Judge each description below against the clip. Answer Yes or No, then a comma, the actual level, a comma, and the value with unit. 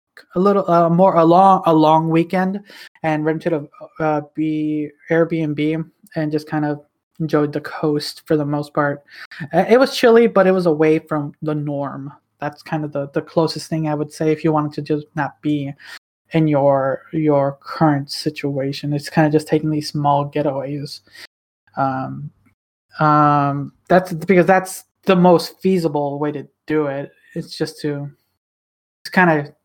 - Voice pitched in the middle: Yes, medium, 155 Hz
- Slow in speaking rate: No, average, 170 wpm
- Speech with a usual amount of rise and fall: No, narrow, 2.2 semitones